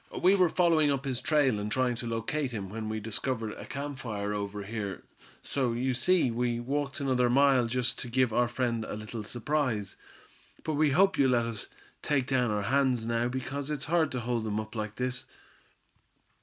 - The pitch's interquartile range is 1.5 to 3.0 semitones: No, average, 3.7 semitones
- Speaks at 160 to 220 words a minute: Yes, average, 195 wpm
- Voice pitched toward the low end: Yes, low, 125 Hz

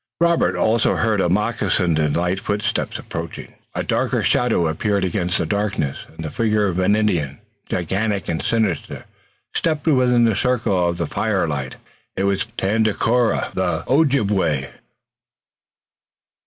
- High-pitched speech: No, low, 100 Hz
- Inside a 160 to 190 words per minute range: No, average, 140 wpm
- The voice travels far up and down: No, average, 4.6 semitones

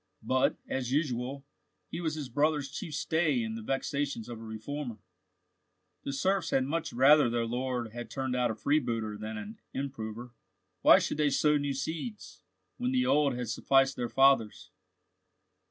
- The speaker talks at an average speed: Yes, average, 165 wpm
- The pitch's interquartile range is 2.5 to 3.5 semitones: No, average, 3.9 semitones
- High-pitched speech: No, low, 135 Hz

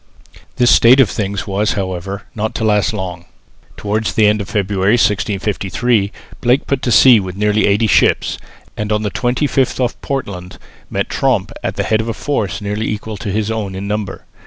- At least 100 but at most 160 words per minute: No, average, 185 wpm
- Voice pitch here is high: No, low, 105 Hz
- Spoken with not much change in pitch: Yes, narrow, 2.3 semitones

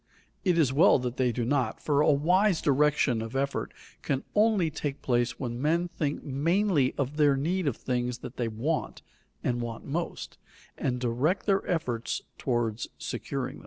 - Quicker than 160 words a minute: Yes, average, 170 wpm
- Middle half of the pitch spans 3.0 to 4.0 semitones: No, average, 4.8 semitones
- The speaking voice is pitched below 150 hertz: Yes, medium, 140 Hz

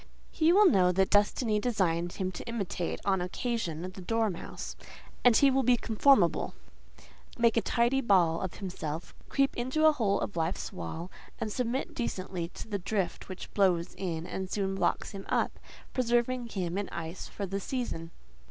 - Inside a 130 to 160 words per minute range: No, average, 170 wpm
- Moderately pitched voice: No, high, 200 Hz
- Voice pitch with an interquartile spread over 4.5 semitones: Yes, average, 5.0 semitones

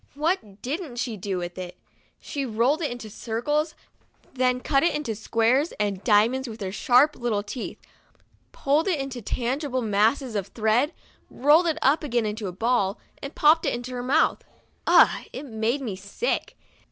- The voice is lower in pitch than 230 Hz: No, high, 245 Hz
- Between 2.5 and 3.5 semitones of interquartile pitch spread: No, average, 4.9 semitones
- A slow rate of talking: No, average, 175 wpm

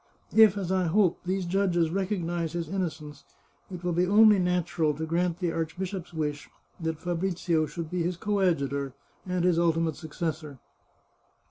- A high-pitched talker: No, medium, 175 Hz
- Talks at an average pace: Yes, average, 150 wpm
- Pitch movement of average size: No, narrow, 2.2 semitones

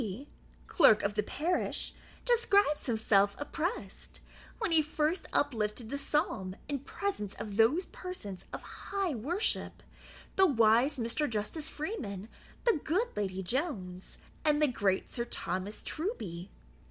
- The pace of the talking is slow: Yes, slow, 130 wpm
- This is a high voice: Yes, very high, 265 Hz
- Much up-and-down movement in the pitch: Yes, wide, 7.9 semitones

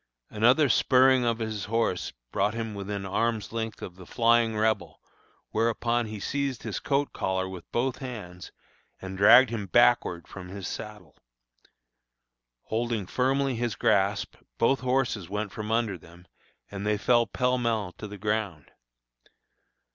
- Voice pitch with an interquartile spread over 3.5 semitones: No, average, 3.2 semitones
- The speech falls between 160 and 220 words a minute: No, average, 145 wpm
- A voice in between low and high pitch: No, low, 110 Hz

